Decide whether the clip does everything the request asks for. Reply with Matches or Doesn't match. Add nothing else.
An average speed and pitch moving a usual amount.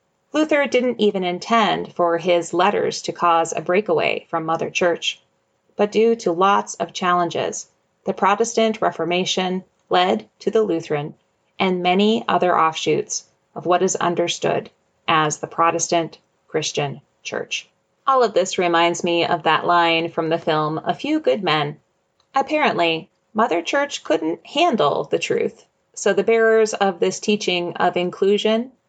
Matches